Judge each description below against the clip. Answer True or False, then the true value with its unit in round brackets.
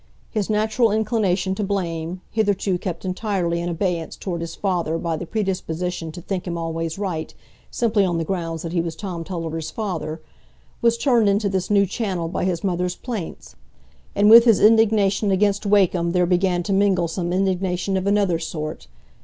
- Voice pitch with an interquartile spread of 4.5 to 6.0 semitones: False (3.1 semitones)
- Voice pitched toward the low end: False (185 Hz)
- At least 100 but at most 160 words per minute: False (175 wpm)